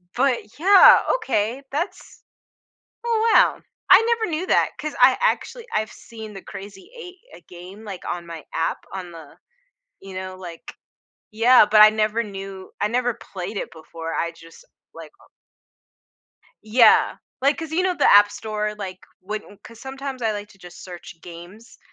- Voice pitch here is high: Yes, high, 215 Hz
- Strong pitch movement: Yes, wide, 6.0 semitones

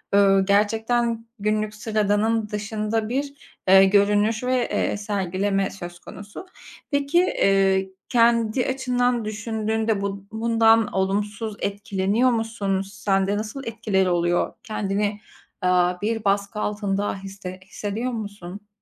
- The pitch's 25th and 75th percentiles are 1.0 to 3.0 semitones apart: Yes, narrow, 2.4 semitones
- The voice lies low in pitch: No, high, 210 Hz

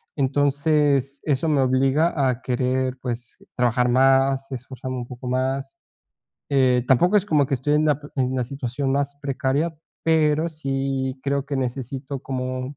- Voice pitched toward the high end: No, low, 135 Hz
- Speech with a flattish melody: Yes, narrow, 1.8 semitones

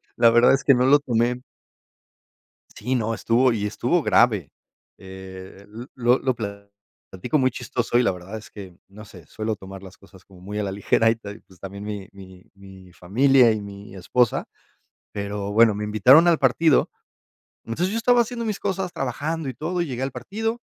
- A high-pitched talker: No, low, 115 Hz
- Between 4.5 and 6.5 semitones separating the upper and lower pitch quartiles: Yes, average, 5.0 semitones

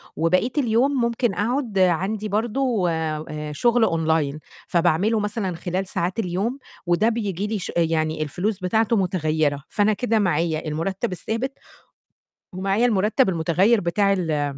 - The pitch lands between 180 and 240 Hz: Yes, high, 190 Hz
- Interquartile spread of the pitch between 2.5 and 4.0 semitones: No, average, 5.1 semitones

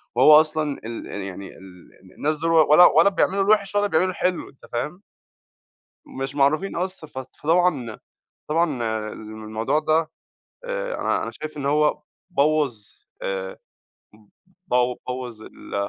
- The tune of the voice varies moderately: No, wide, 5.8 semitones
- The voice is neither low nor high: Yes, medium, 150 Hz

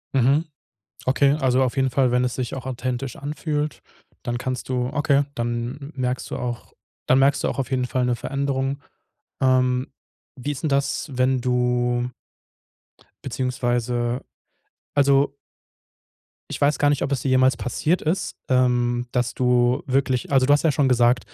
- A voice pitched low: Yes, low, 130 Hz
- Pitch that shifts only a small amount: Yes, narrow, 2.0 semitones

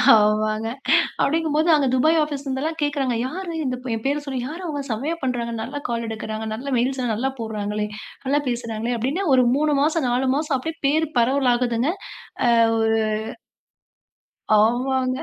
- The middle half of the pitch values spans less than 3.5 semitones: No, average, 4.1 semitones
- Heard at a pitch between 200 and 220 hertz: No, very high, 260 Hz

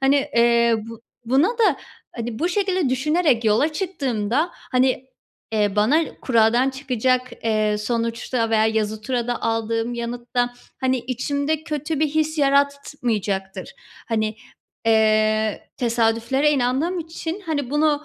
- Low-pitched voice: No, very high, 250 Hz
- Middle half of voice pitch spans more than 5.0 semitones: No, average, 4.4 semitones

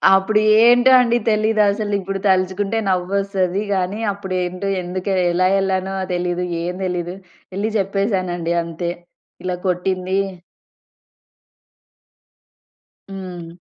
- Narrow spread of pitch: Yes, narrow, 1.9 semitones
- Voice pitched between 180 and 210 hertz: Yes, high, 190 Hz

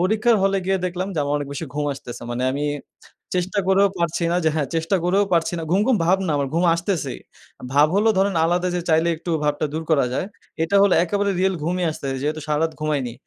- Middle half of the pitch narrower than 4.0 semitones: No, average, 4.3 semitones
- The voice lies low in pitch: No, medium, 170 Hz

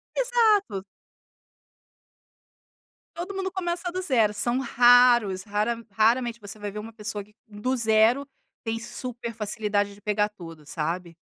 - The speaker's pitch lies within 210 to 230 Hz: Yes, high, 225 Hz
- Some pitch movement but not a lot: Yes, average, 3.4 semitones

